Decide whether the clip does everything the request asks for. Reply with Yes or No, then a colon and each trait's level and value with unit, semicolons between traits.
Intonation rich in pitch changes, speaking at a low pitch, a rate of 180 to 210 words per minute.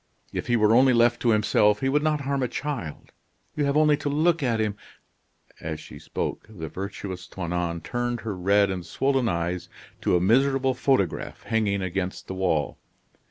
Yes: wide, 6.3 semitones; low, 110 Hz; average, 185 wpm